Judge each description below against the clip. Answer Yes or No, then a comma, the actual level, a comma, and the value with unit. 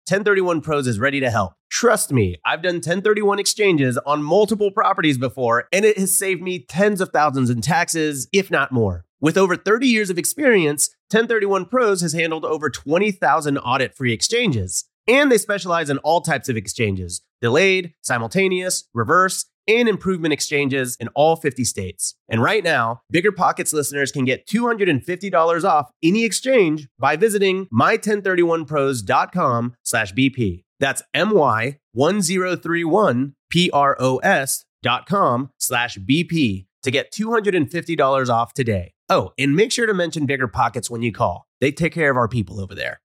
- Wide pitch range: Yes, wide, 6.9 semitones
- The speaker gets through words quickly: No, average, 145 wpm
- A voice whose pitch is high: No, medium, 155 Hz